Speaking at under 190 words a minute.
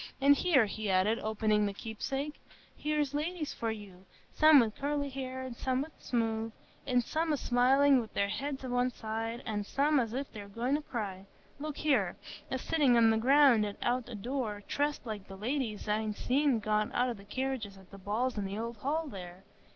No: average, 195 wpm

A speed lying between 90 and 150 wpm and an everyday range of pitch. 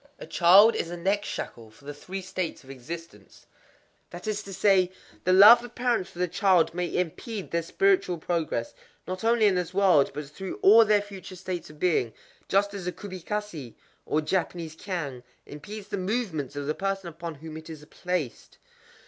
No: average, 180 wpm; average, 3.9 semitones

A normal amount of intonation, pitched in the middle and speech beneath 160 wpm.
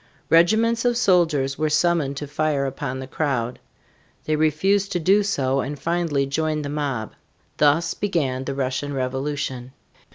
Yes: average, 3.9 semitones; medium, 145 Hz; average, 150 wpm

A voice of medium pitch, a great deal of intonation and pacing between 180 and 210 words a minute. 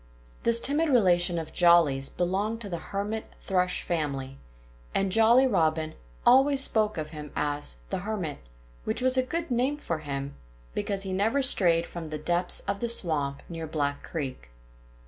No: medium, 180 Hz; wide, 6.3 semitones; average, 165 wpm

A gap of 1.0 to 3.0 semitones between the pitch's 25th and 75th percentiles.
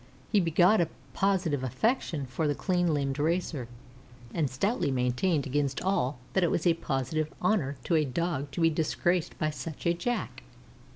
No: average, 4.2 semitones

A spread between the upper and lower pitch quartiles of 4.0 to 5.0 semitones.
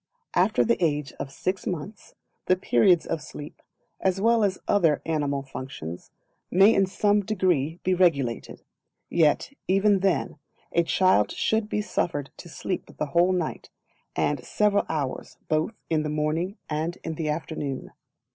Yes: average, 4.5 semitones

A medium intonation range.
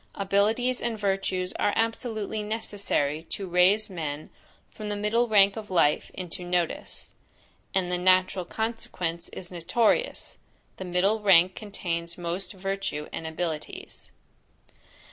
Yes: average, 3.2 semitones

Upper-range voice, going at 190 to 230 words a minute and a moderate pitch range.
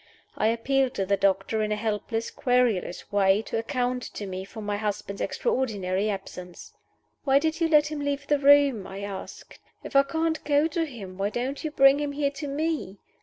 No: high, 245 Hz; average, 195 wpm; wide, 6.0 semitones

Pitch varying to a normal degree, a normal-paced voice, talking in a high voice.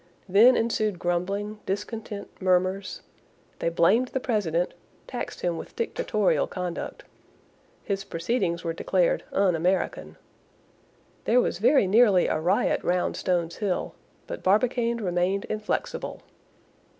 No: average, 4.0 semitones; slow, 115 wpm; high, 195 Hz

